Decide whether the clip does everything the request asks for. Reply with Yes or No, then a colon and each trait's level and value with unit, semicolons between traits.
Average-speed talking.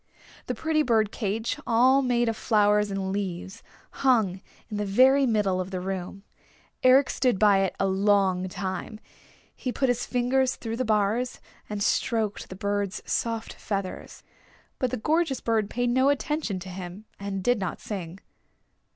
Yes: average, 160 wpm